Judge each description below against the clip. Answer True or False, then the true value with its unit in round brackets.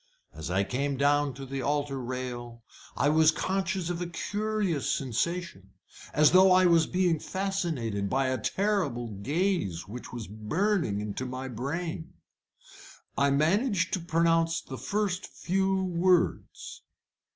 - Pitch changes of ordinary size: False (6.2 semitones)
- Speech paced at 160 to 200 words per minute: False (135 wpm)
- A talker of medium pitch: True (155 Hz)